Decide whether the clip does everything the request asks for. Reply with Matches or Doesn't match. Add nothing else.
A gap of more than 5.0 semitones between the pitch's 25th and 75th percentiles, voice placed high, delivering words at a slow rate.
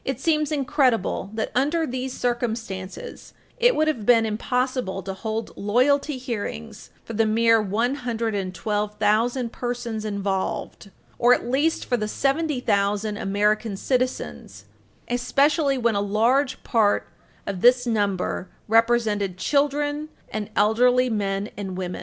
Doesn't match